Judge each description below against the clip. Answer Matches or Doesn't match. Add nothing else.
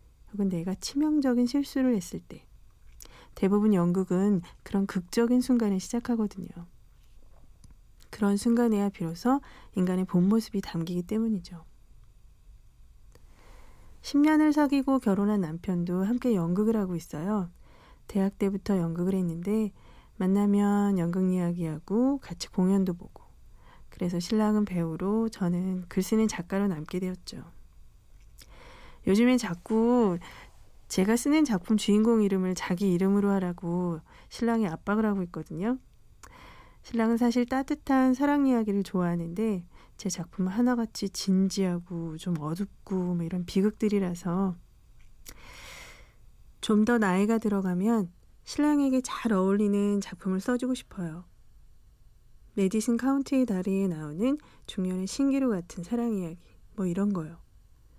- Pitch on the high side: Matches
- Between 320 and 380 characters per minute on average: Doesn't match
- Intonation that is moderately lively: Matches